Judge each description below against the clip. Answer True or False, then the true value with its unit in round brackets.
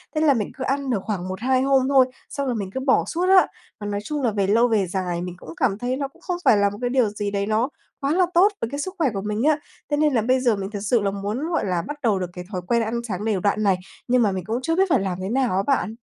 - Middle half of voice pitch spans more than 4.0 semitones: True (5.2 semitones)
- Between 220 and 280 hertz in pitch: True (230 Hz)